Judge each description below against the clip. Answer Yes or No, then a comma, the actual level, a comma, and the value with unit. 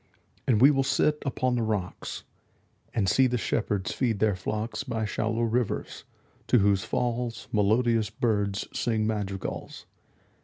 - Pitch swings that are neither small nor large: Yes, average, 3.0 semitones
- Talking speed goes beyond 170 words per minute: No, average, 145 wpm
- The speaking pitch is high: No, low, 110 Hz